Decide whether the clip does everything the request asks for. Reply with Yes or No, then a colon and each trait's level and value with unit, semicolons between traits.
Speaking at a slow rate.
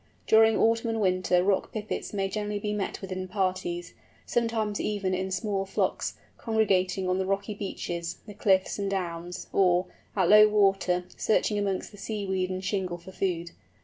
No: average, 170 wpm